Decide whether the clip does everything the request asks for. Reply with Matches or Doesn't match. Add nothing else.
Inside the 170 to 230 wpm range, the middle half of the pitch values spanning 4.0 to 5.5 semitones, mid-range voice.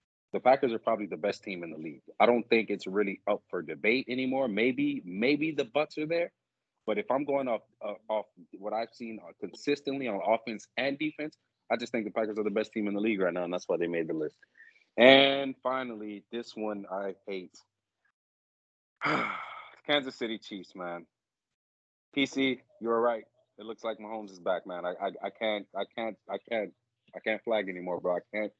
Doesn't match